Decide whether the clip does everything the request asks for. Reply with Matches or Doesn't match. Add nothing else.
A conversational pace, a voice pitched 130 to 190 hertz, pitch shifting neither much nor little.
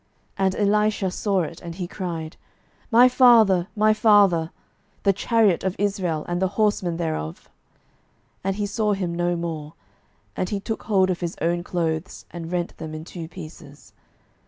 Matches